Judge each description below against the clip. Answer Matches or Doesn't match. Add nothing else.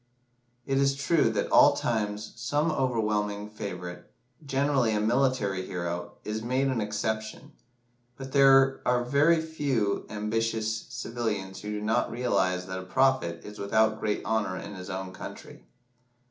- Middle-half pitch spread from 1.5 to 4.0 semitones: Doesn't match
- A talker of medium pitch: Doesn't match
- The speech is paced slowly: Doesn't match